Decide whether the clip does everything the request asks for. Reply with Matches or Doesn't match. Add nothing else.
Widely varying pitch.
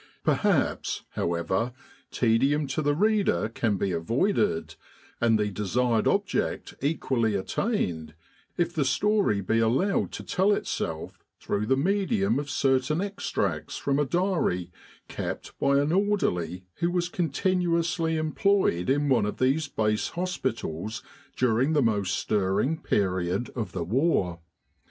Matches